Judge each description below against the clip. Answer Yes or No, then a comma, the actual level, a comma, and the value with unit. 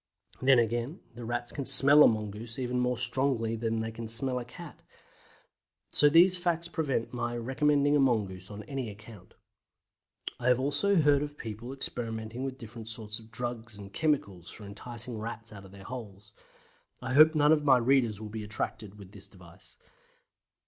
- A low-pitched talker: Yes, low, 120 Hz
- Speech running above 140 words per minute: Yes, average, 175 wpm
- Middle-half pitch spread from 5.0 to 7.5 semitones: No, average, 3.8 semitones